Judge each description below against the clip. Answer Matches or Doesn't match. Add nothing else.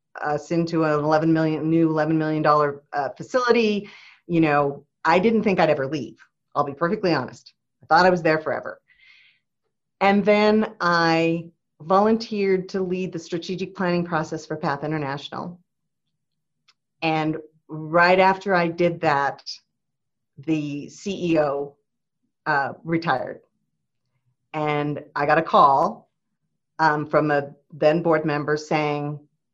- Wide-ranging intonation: Doesn't match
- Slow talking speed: Matches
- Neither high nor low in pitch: Matches